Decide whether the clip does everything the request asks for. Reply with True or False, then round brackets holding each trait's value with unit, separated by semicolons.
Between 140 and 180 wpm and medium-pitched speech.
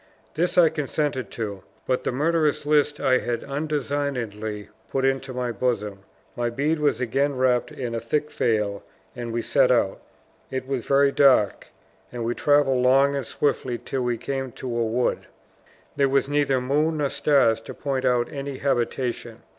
False (170 wpm; 130 Hz)